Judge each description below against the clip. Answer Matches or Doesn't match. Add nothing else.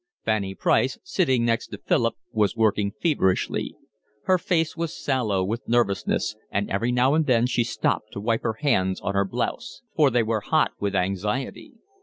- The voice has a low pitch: Matches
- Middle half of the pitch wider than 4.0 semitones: Matches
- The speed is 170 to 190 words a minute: Matches